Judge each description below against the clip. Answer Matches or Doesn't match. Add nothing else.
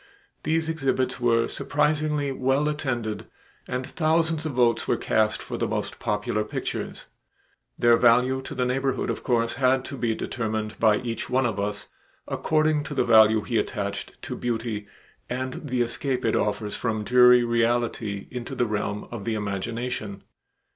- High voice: Doesn't match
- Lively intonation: Doesn't match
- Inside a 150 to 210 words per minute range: Matches